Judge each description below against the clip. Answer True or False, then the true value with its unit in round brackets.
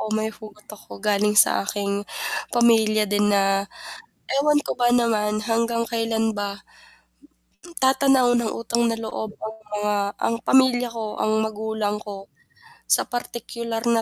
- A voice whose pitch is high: True (225 Hz)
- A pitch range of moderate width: False (2.0 semitones)